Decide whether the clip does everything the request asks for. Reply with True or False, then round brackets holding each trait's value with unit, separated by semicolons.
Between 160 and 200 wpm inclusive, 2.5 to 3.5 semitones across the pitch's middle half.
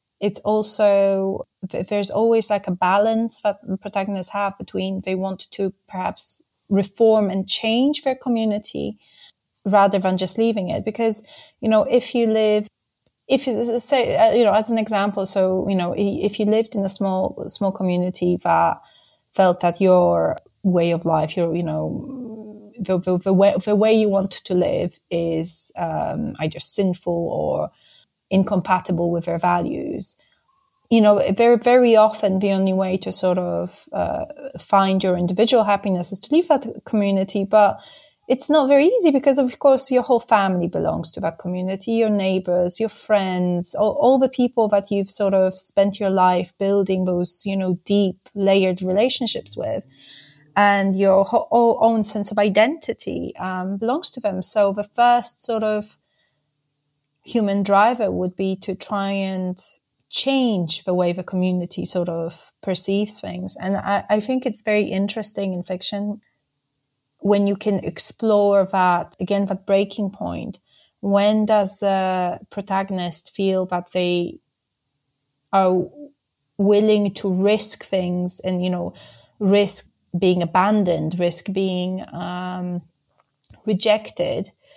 False (150 wpm; 2.9 semitones)